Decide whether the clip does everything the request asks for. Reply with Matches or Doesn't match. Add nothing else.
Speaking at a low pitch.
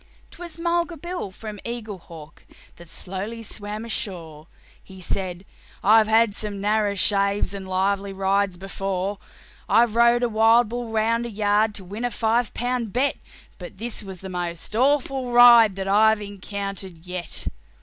Doesn't match